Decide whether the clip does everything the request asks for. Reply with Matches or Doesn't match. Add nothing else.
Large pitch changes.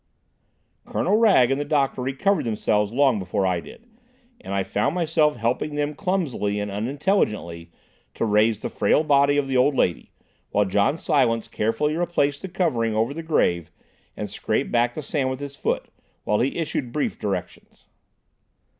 Matches